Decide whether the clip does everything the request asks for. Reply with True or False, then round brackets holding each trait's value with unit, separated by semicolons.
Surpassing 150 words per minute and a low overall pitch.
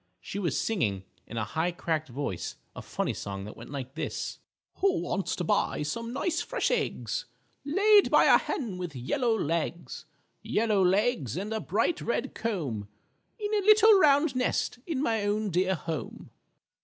False (170 wpm; 205 Hz)